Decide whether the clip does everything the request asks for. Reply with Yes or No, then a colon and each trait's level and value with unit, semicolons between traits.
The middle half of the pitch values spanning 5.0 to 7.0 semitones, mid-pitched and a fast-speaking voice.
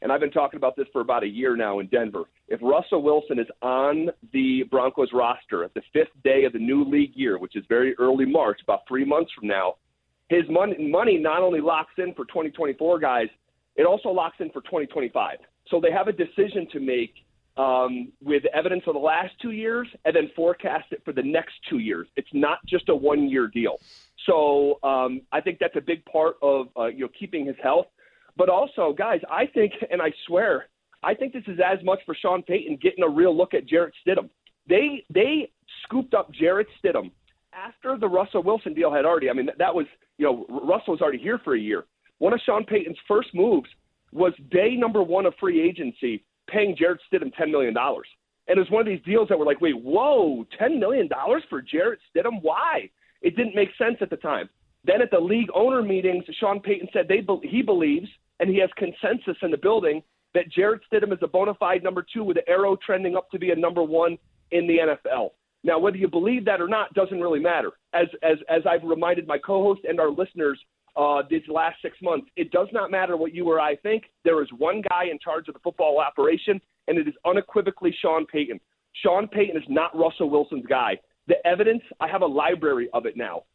Yes: wide, 5.4 semitones; medium, 180 Hz; fast, 220 wpm